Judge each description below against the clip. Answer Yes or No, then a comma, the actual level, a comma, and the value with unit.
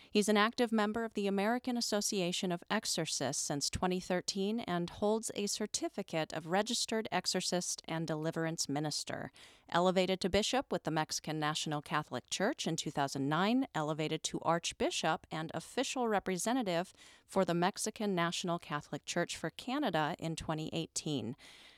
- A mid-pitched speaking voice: Yes, medium, 180 Hz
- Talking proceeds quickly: No, slow, 135 wpm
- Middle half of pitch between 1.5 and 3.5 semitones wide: No, average, 4.7 semitones